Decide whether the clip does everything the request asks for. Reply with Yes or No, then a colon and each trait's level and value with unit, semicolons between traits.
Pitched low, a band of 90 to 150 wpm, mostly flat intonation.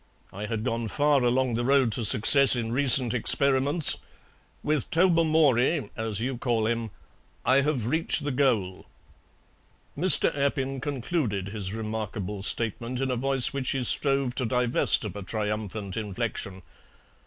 No: low, 125 Hz; average, 140 wpm; average, 3.9 semitones